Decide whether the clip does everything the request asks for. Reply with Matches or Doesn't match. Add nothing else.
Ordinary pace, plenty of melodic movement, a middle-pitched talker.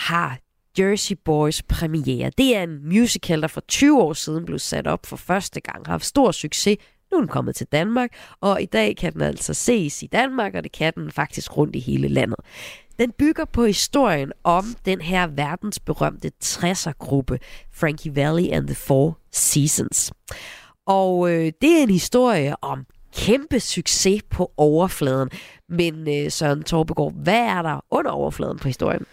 Matches